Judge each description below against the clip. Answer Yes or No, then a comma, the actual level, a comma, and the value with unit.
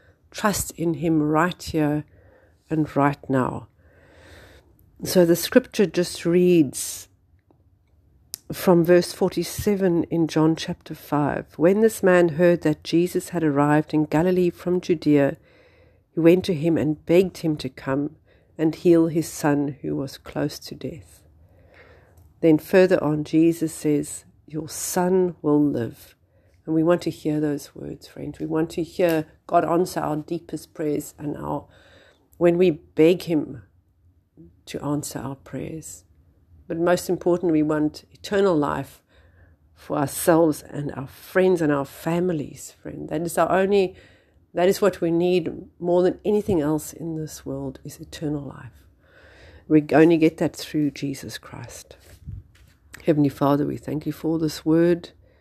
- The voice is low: No, medium, 155 Hz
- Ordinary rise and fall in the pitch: Yes, average, 4.4 semitones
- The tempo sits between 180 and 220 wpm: No, average, 145 wpm